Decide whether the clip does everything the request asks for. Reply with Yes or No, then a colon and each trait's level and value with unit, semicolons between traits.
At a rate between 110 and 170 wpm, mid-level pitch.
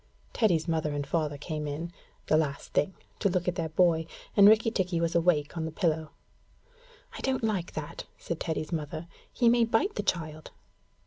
No: average, 185 wpm; medium, 165 Hz